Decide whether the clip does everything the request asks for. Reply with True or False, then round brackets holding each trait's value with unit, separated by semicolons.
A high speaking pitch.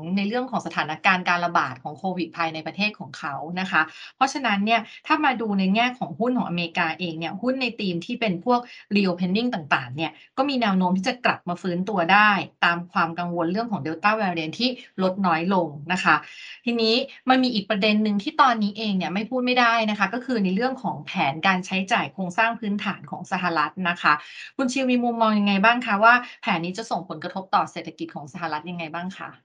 True (195 Hz)